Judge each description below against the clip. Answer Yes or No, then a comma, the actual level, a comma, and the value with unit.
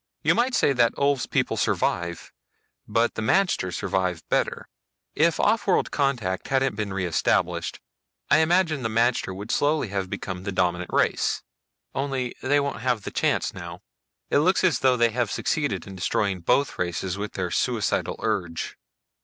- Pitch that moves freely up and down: Yes, wide, 7.0 semitones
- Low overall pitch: Yes, low, 115 Hz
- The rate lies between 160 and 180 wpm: Yes, average, 165 wpm